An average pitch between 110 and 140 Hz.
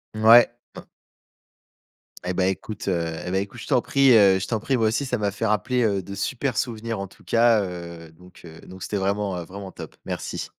No: low, 100 Hz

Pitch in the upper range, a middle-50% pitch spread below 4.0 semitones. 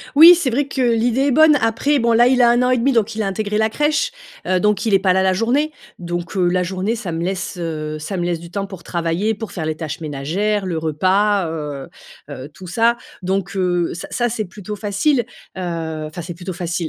No: high, 195 Hz; average, 5.1 semitones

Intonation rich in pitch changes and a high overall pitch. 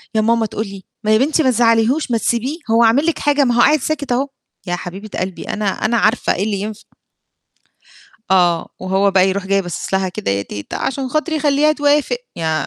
Yes: wide, 6.3 semitones; high, 225 Hz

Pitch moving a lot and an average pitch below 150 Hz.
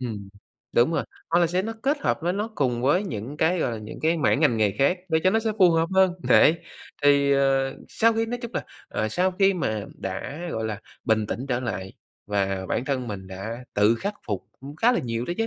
Yes: wide, 8.4 semitones; low, 135 Hz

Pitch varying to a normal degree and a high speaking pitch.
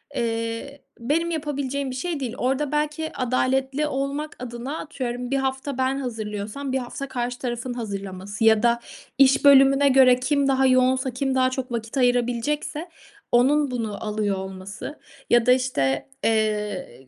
Yes: average, 3.2 semitones; very high, 255 Hz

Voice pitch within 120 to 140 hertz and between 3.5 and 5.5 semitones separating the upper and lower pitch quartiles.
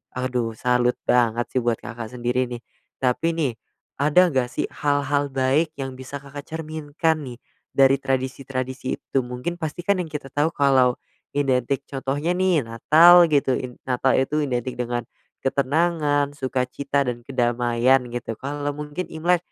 No: low, 135 Hz; average, 3.0 semitones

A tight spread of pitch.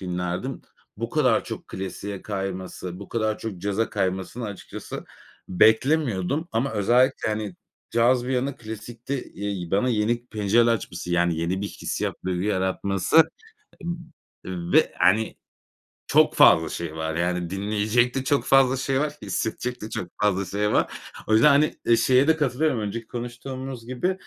No: average, 4.8 semitones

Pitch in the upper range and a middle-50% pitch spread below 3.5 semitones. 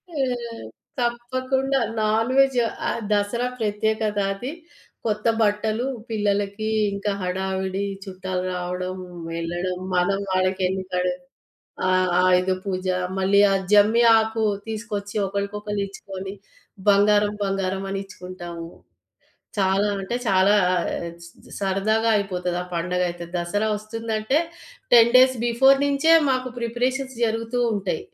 Yes: high, 205 Hz; average, 3.1 semitones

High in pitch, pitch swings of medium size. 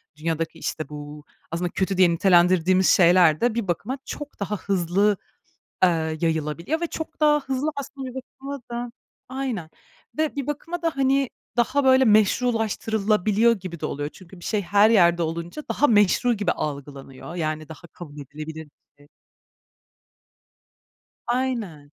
No: high, 195 Hz; wide, 7.3 semitones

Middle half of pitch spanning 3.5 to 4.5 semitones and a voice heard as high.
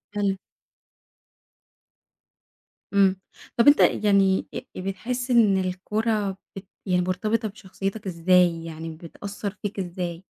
No: narrow, 2.5 semitones; high, 195 Hz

